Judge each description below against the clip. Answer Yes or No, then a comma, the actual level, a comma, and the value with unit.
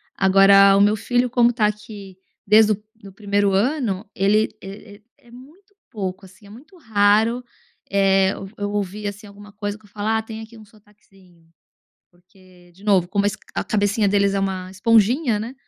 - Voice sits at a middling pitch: No, high, 205 Hz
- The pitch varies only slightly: Yes, narrow, 2.1 semitones